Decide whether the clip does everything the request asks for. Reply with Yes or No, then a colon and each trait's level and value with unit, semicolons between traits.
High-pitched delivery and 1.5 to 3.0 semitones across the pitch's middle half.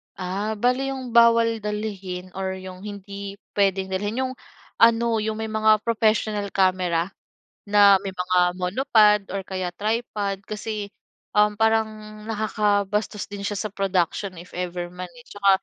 Yes: high, 205 Hz; narrow, 2.4 semitones